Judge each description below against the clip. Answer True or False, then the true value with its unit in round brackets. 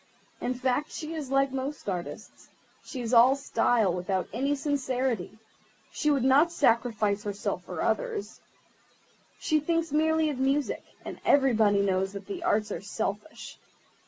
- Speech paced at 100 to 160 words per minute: True (145 wpm)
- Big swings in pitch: True (5.8 semitones)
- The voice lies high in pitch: True (260 Hz)